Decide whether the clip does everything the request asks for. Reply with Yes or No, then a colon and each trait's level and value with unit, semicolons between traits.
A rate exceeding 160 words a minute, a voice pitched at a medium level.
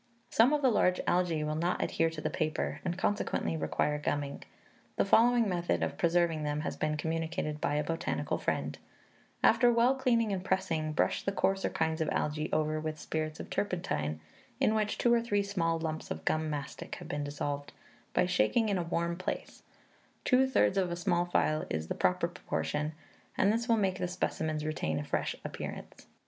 Yes: average, 190 wpm; medium, 165 Hz